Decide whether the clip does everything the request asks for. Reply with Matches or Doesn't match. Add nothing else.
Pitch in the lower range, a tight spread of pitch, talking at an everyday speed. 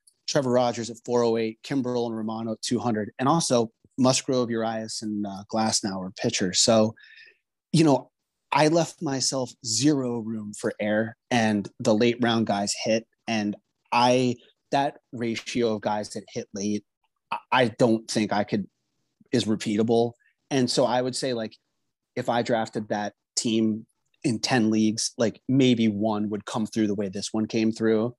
Matches